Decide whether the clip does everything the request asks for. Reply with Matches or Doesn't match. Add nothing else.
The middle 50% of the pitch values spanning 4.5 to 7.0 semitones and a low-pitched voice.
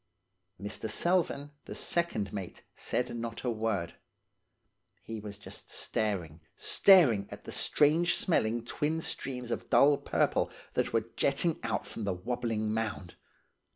Matches